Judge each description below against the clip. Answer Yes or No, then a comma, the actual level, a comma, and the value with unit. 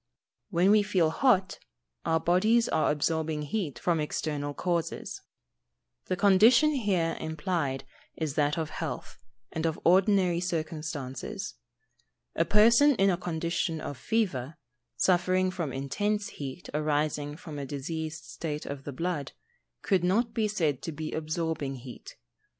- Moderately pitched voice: Yes, medium, 165 Hz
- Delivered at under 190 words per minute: Yes, average, 140 wpm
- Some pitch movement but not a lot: Yes, average, 3.9 semitones